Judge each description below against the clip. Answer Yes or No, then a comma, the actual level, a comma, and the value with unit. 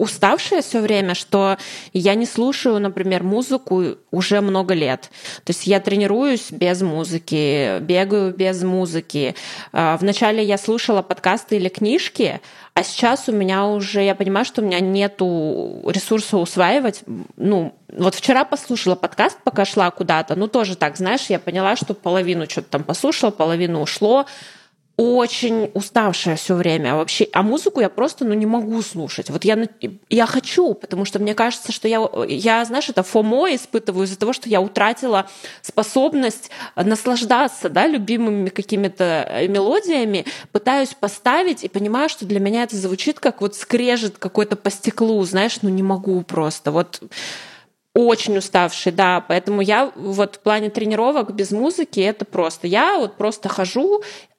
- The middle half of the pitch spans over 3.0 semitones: Yes, average, 3.6 semitones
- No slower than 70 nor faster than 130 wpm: No, average, 150 wpm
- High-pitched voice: Yes, high, 205 Hz